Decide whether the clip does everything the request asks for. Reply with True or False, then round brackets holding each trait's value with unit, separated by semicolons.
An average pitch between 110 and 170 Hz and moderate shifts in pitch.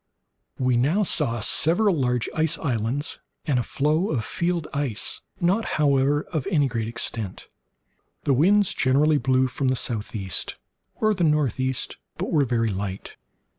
True (135 Hz; 4.7 semitones)